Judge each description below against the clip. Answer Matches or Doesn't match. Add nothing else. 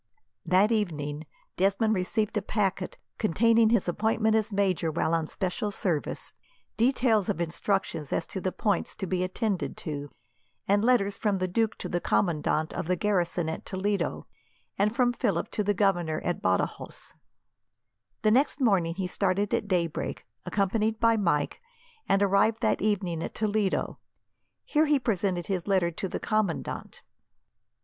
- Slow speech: Doesn't match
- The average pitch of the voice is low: Doesn't match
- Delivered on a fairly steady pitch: Doesn't match